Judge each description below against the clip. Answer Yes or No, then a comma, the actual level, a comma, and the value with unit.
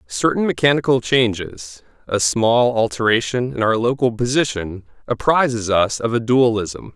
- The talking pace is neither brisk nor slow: No, slow, 130 wpm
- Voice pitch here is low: Yes, low, 115 Hz